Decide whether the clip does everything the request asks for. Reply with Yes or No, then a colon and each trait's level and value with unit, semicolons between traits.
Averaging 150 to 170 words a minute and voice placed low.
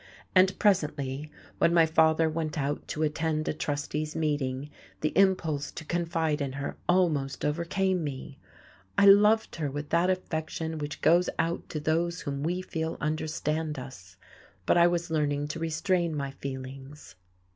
No: average, 155 wpm; medium, 155 Hz